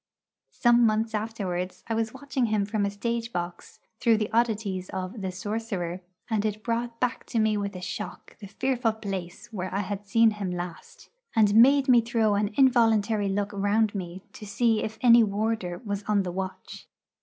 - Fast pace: No, average, 185 wpm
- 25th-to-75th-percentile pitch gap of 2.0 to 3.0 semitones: Yes, narrow, 2.6 semitones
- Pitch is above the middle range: Yes, high, 215 Hz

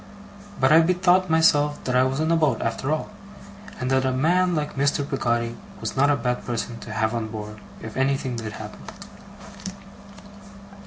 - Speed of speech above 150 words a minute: Yes, average, 175 wpm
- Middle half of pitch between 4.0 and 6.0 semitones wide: Yes, average, 4.7 semitones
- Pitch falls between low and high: No, low, 130 Hz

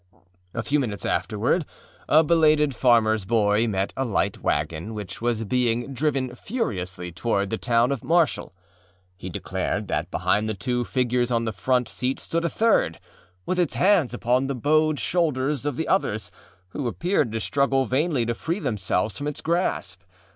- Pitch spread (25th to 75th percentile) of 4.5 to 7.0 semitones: Yes, wide, 5.4 semitones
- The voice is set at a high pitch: No, low, 125 Hz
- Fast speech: No, average, 170 wpm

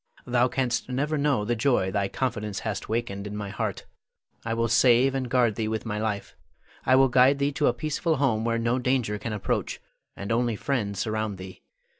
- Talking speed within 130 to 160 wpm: No, average, 200 wpm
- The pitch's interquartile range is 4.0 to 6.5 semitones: No, average, 3.5 semitones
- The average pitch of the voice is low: Yes, low, 115 Hz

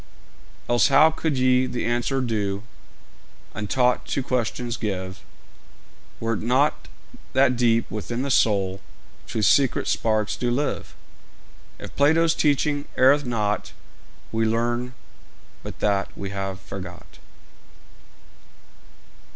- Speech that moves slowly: Yes, slow, 110 wpm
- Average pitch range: Yes, average, 3.7 semitones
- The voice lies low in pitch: Yes, low, 120 Hz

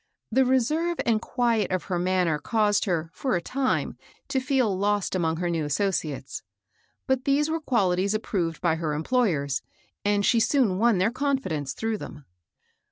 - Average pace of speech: Yes, average, 170 wpm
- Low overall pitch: No, high, 205 Hz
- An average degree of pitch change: No, wide, 6.6 semitones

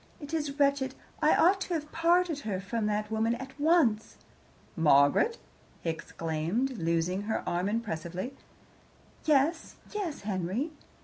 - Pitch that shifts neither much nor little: No, wide, 8.4 semitones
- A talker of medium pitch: No, high, 230 Hz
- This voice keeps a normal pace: No, slow, 130 wpm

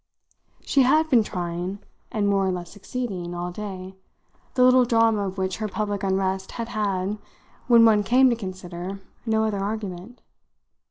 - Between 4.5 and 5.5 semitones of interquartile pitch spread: No, average, 3.3 semitones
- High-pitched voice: Yes, high, 200 Hz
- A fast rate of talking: No, average, 155 wpm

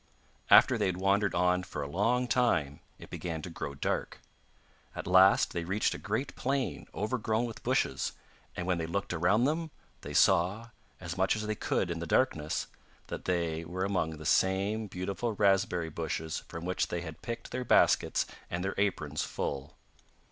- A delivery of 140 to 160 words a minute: No, average, 175 wpm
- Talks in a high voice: No, very low, 95 Hz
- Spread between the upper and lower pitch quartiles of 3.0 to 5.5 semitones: Yes, average, 4.2 semitones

